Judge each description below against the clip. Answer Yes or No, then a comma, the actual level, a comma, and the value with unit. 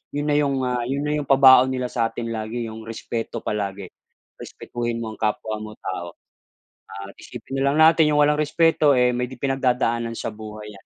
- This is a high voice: No, low, 120 Hz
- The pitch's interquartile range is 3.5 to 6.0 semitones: Yes, average, 3.8 semitones